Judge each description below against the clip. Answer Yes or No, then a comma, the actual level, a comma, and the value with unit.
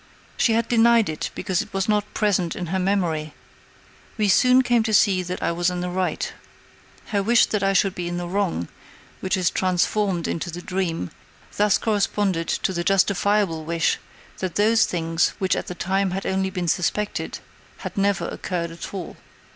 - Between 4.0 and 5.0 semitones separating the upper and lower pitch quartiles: No, average, 2.8 semitones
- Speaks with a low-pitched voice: No, high, 190 Hz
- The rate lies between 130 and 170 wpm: No, average, 185 wpm